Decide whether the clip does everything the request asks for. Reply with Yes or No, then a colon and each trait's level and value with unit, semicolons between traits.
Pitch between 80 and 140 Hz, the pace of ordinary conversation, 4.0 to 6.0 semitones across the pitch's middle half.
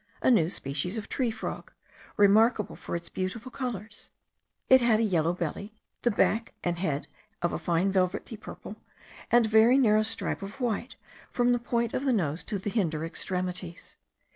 No: high, 210 Hz; average, 175 wpm; average, 4.6 semitones